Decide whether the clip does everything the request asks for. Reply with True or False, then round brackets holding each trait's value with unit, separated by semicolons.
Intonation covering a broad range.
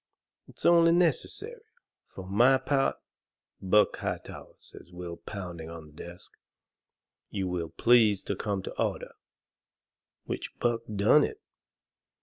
True (6.9 semitones)